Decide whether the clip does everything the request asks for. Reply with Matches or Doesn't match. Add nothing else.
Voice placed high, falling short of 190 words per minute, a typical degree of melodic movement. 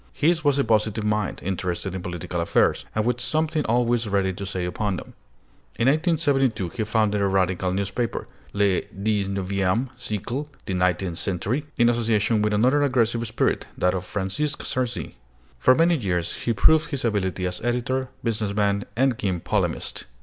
Doesn't match